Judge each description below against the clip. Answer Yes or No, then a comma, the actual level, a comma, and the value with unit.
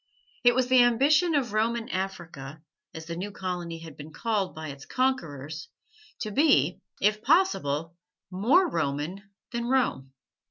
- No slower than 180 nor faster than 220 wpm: No, average, 145 wpm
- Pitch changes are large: Yes, wide, 7.4 semitones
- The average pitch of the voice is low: No, high, 195 Hz